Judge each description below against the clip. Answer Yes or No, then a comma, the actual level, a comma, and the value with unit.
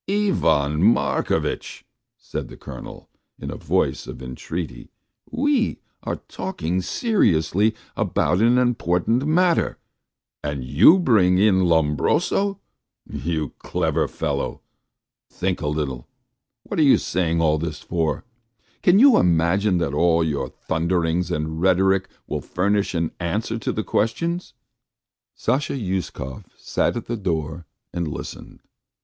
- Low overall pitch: Yes, very low, 90 Hz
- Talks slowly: Yes, slow, 125 wpm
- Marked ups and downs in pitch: Yes, wide, 6.3 semitones